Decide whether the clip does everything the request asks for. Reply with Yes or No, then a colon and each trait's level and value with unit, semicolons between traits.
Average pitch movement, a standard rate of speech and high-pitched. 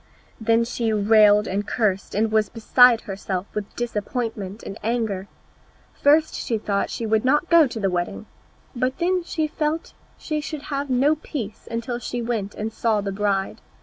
Yes: average, 3.9 semitones; average, 170 wpm; high, 225 Hz